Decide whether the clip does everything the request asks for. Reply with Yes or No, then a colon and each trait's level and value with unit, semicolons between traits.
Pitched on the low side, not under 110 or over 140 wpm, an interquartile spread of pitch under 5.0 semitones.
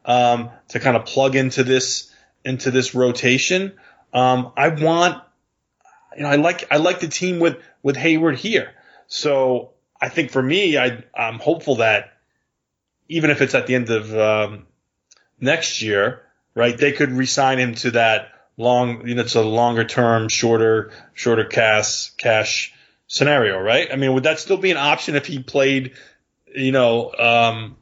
No: low, 130 Hz; average, 170 wpm; average, 3.5 semitones